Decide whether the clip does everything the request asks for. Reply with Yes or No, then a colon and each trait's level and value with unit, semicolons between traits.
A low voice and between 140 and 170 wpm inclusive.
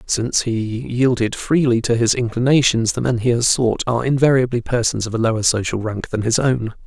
No: low, 120 Hz; average, 200 wpm